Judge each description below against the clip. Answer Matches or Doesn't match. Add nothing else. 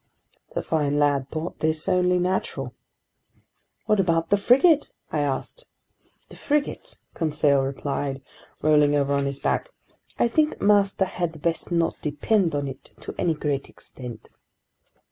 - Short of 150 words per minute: Matches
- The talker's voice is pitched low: Doesn't match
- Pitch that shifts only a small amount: Doesn't match